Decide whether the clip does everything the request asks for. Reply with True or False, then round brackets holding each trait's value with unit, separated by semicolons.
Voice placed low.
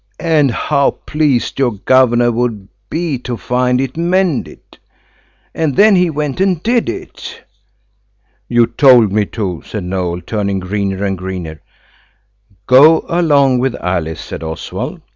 True (125 Hz)